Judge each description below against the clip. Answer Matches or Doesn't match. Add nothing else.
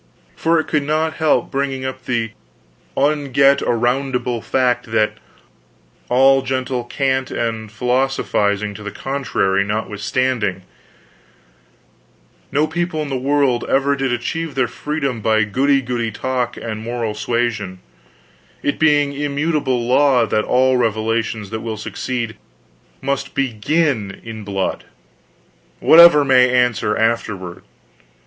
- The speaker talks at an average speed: Doesn't match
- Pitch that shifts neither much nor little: Matches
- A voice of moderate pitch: Doesn't match